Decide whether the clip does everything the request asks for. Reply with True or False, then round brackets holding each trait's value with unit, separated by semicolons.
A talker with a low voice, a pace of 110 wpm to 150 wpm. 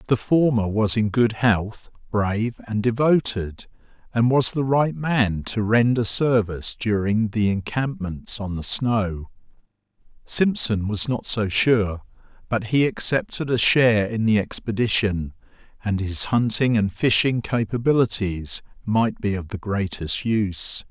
True (110 Hz; 140 wpm)